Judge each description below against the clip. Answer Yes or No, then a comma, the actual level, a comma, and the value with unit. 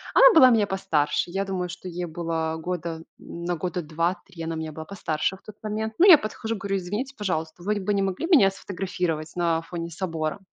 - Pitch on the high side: No, medium, 180 Hz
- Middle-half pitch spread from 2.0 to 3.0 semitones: No, average, 3.4 semitones